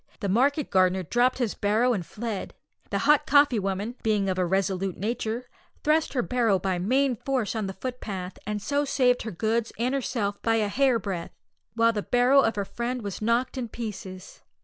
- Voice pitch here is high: Yes, high, 225 Hz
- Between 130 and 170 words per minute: No, average, 190 wpm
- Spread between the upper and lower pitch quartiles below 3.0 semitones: No, average, 4.2 semitones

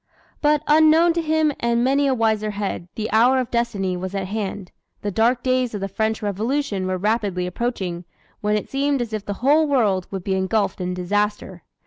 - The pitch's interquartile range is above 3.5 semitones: Yes, average, 4.8 semitones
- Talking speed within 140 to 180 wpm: No, average, 195 wpm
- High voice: Yes, high, 220 Hz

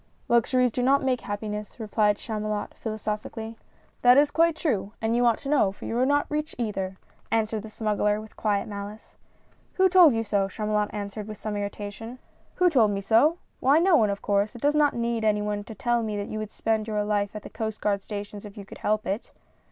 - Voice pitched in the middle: No, high, 215 Hz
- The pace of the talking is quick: Yes, fast, 235 wpm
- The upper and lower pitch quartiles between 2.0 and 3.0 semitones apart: Yes, average, 2.7 semitones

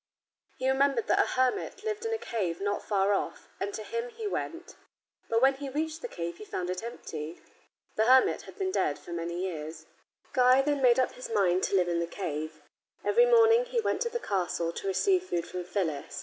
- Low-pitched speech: No, high, 230 Hz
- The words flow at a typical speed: No, fast, 210 wpm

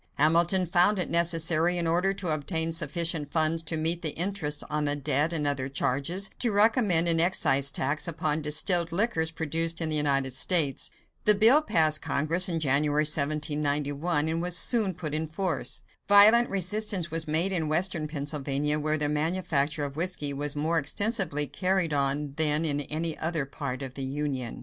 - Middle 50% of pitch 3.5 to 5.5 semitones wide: No, average, 3.1 semitones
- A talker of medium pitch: Yes, medium, 160 Hz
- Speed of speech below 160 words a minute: No, average, 175 wpm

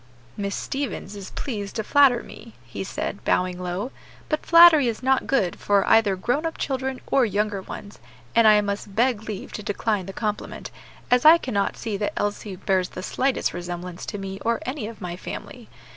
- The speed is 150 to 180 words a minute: No, average, 190 wpm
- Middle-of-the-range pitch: No, high, 210 Hz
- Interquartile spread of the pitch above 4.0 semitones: Yes, average, 4.4 semitones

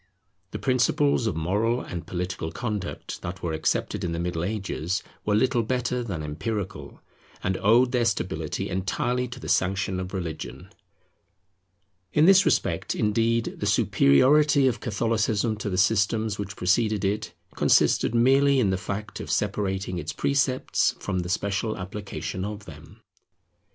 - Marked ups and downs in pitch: No, average, 4.3 semitones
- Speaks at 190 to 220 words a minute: No, average, 145 wpm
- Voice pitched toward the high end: No, low, 105 Hz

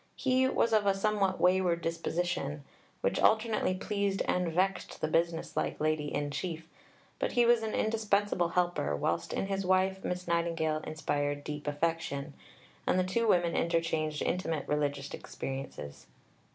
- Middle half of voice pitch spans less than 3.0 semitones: No, average, 4.2 semitones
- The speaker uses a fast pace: No, average, 150 wpm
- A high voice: No, medium, 170 Hz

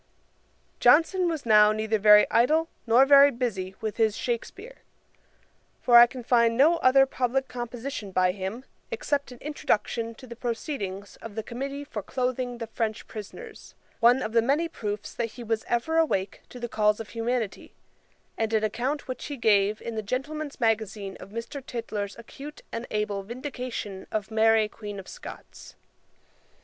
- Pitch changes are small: No, average, 3.7 semitones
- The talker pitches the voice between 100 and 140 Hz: No, high, 235 Hz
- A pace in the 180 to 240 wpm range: No, average, 165 wpm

